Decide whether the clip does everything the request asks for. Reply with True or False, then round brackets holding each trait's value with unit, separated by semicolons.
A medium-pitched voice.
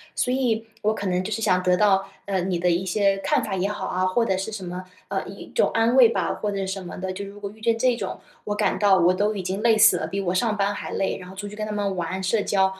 False (200 Hz)